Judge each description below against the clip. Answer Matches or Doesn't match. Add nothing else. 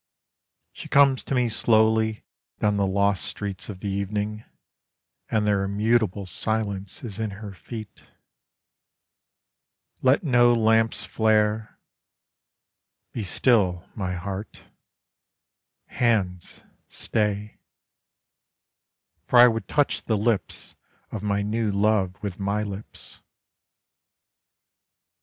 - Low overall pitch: Matches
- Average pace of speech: Doesn't match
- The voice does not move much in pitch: Matches